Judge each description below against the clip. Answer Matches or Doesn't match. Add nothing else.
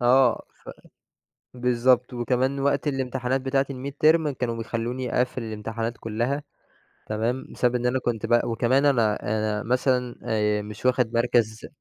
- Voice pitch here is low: Matches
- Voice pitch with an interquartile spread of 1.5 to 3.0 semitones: Matches